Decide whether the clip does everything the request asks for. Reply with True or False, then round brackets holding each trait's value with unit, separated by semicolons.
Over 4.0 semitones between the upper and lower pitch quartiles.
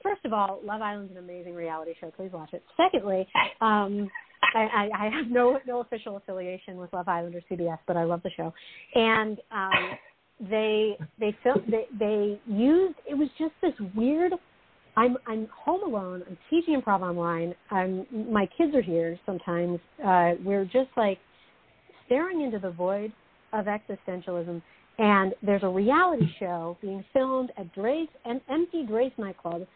True (5.1 semitones)